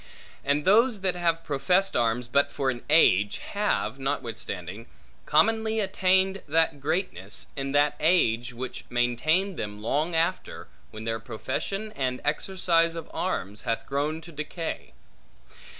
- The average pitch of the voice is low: No, medium, 150 Hz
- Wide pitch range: Yes, wide, 6.9 semitones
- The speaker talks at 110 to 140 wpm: Yes, slow, 135 wpm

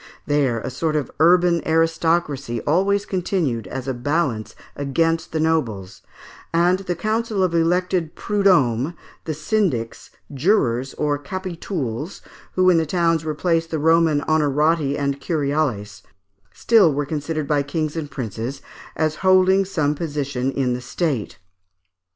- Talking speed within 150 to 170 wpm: No, slow, 135 wpm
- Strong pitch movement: No, average, 3.9 semitones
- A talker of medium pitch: Yes, medium, 155 Hz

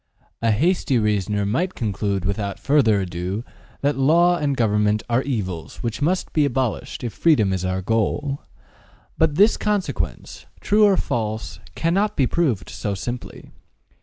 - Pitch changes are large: Yes, wide, 6.8 semitones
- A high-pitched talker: No, low, 120 Hz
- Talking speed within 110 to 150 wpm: Yes, average, 145 wpm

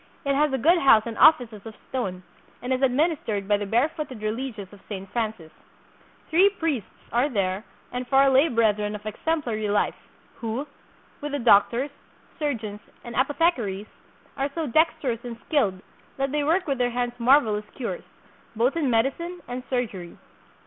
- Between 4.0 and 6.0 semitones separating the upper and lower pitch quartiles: Yes, average, 5.0 semitones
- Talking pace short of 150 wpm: No, average, 165 wpm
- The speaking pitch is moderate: No, high, 245 Hz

